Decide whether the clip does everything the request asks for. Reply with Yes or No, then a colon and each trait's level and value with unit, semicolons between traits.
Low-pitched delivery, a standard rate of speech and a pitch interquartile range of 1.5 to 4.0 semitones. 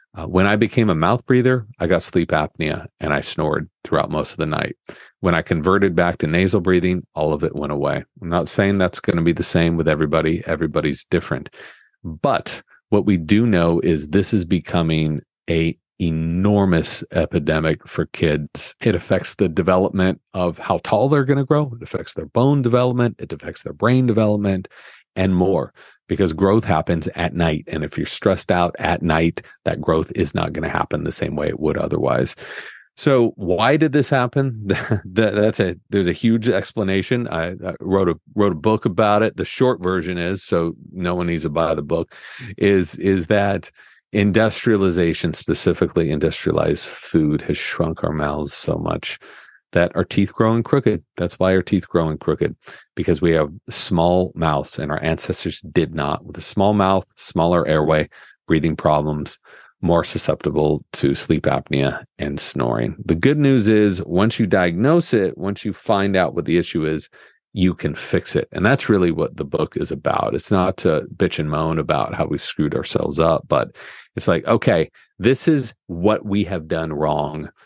No: very low, 95 Hz; average, 185 wpm; average, 4.7 semitones